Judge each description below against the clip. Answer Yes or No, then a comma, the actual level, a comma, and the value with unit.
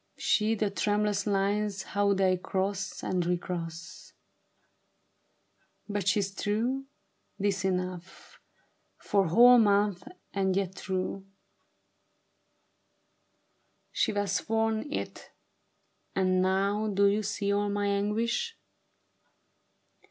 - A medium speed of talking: No, slow, 95 wpm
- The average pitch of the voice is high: Yes, high, 200 Hz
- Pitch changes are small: Yes, narrow, 1.8 semitones